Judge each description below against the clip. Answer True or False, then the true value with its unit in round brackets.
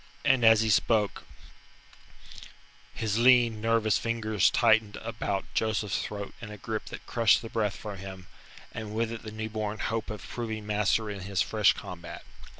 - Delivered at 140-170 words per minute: True (165 wpm)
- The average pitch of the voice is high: False (110 Hz)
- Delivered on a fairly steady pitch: True (1.5 semitones)